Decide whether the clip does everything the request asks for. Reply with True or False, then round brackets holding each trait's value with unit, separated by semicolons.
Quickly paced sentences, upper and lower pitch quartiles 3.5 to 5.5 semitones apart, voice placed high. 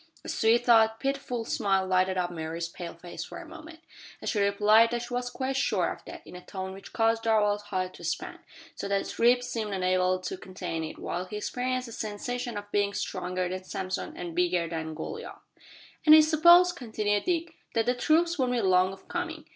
True (210 wpm; 5.1 semitones; 210 Hz)